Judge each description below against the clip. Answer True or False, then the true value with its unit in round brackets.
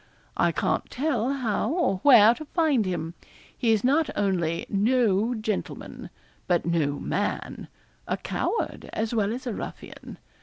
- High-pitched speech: True (220 Hz)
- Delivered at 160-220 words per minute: False (145 wpm)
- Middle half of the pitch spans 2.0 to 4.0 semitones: False (5.0 semitones)